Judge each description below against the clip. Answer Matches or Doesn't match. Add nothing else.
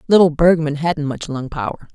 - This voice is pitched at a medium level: Matches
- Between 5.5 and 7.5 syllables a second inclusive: Doesn't match